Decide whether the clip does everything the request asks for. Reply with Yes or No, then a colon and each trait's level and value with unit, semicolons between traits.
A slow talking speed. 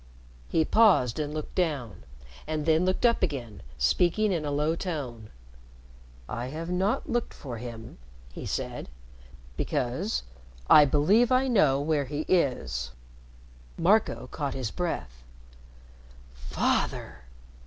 Yes: slow, 120 wpm